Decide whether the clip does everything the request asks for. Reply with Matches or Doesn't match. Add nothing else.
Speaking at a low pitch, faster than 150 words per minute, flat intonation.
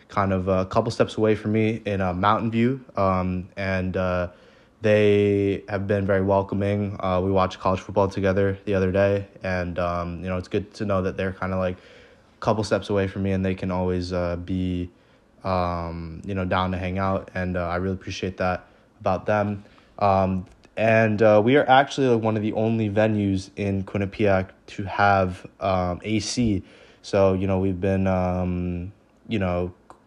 Matches